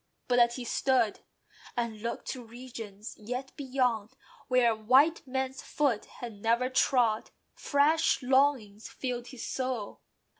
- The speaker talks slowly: Yes, slow, 125 wpm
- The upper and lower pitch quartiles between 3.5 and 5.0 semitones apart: No, narrow, 2.6 semitones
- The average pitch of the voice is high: Yes, very high, 250 Hz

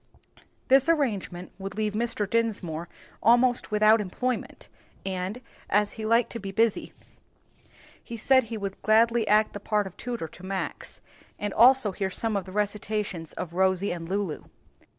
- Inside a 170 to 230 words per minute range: No, average, 155 wpm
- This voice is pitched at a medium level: No, high, 210 Hz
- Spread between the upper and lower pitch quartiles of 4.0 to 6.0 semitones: No, average, 3.3 semitones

